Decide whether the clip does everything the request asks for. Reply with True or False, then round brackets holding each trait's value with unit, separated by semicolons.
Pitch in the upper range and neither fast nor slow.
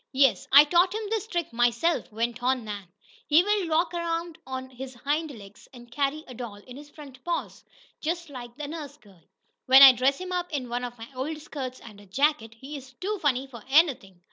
False (270 Hz; 215 wpm)